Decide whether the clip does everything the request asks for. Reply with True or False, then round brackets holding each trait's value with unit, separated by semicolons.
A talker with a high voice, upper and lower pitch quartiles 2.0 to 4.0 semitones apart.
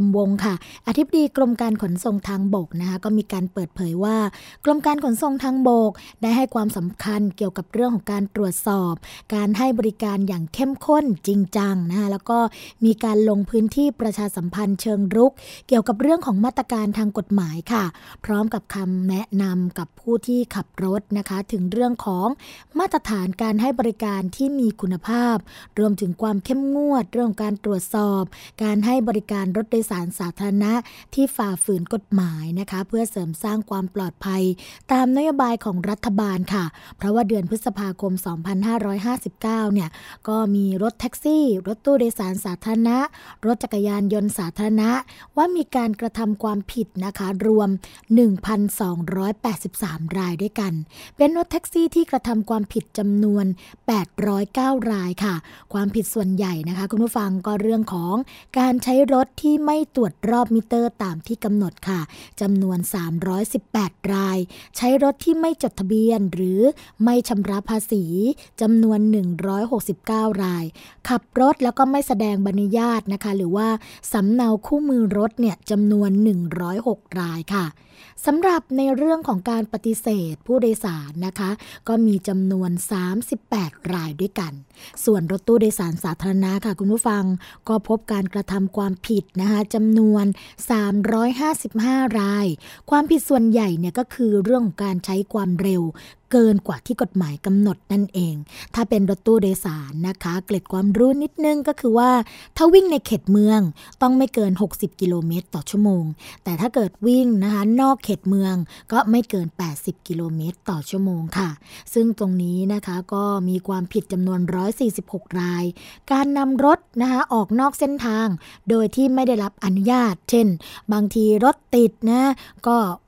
True (210 Hz; 3.5 semitones)